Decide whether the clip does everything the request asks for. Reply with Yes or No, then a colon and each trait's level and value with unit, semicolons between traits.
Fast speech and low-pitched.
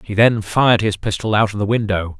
Yes: fast, 245 wpm; low, 105 Hz